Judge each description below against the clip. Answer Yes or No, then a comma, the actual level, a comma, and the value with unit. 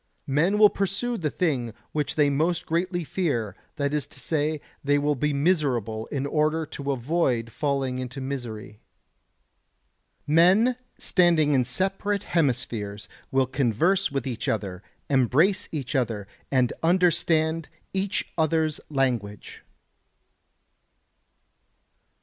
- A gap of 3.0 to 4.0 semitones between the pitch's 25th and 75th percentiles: No, average, 4.9 semitones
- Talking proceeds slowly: Yes, slow, 115 wpm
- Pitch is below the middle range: No, medium, 145 Hz